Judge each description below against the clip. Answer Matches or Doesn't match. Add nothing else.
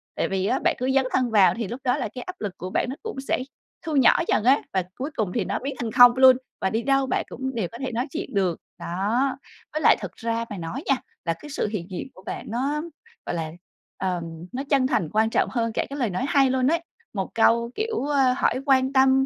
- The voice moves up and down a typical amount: Matches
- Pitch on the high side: Matches